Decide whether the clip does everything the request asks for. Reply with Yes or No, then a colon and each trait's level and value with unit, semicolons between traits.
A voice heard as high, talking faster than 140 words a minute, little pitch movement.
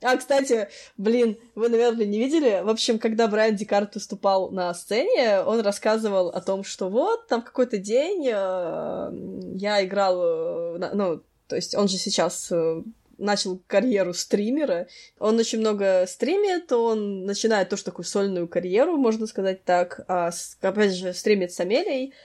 No: high, 210 Hz; average, 150 wpm; average, 3.8 semitones